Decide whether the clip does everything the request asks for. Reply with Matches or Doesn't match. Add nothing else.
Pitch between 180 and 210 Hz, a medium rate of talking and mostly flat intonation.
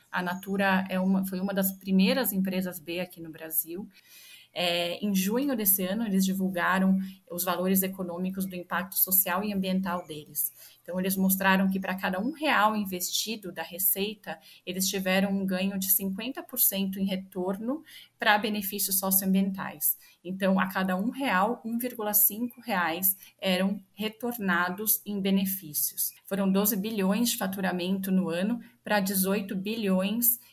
Matches